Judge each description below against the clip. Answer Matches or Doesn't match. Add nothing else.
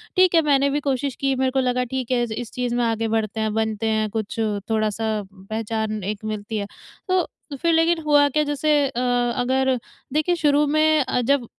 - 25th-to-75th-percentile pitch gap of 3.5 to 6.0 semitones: Matches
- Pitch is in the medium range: Doesn't match